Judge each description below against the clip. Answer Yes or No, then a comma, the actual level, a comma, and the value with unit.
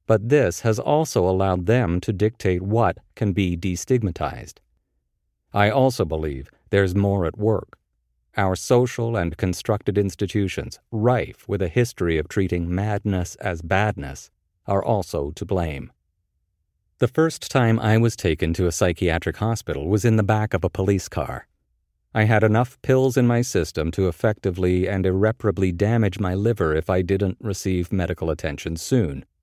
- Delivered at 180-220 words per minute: No, average, 155 wpm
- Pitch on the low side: Yes, very low, 95 Hz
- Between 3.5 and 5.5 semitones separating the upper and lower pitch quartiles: Yes, average, 4.1 semitones